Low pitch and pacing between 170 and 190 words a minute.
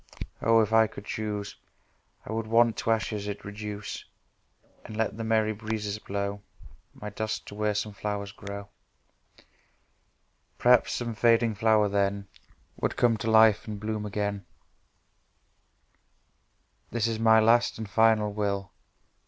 No: low, 105 Hz; slow, 135 wpm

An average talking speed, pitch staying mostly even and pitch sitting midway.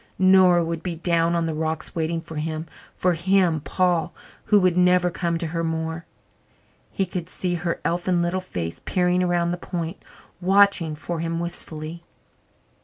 Yes: average, 165 wpm; narrow, 1.7 semitones; medium, 170 Hz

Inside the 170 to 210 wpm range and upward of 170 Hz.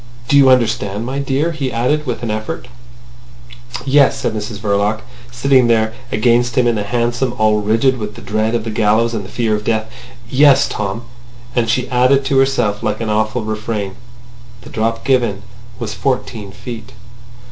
No: average, 175 wpm; low, 115 Hz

